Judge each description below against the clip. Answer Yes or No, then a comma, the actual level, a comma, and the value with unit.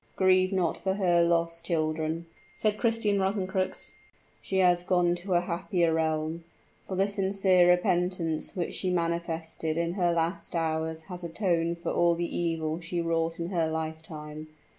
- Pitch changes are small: Yes, narrow, 2.2 semitones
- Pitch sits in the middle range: Yes, medium, 170 Hz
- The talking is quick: No, average, 155 wpm